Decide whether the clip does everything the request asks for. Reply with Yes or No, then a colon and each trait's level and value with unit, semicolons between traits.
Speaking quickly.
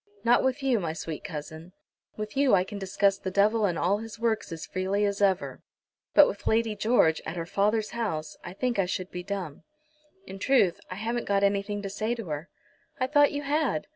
Yes: fast, 210 wpm